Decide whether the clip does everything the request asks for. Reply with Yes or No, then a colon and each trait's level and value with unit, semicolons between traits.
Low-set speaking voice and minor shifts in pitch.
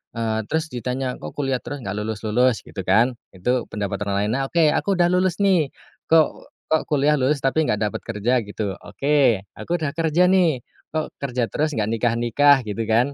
No: low, 130 Hz; wide, 5.6 semitones